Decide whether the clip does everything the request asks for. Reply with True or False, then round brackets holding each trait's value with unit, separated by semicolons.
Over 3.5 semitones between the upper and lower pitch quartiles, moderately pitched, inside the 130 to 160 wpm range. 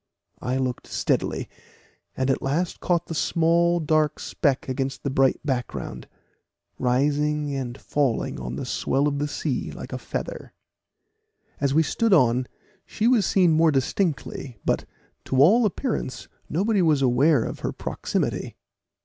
True (4.1 semitones; 145 Hz; 145 wpm)